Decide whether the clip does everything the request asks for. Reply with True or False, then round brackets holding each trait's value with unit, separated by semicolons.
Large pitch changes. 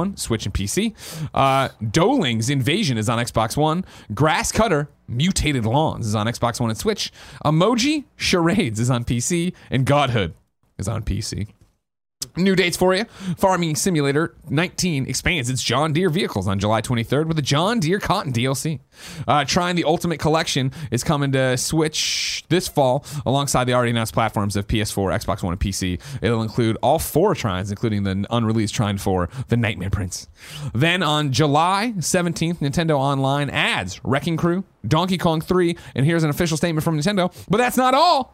True (6.5 semitones)